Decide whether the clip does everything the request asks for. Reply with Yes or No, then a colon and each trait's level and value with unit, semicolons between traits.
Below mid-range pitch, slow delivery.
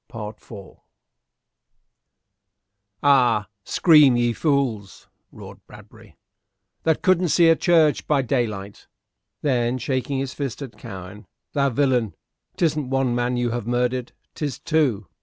Yes: low, 130 Hz; slow, 120 wpm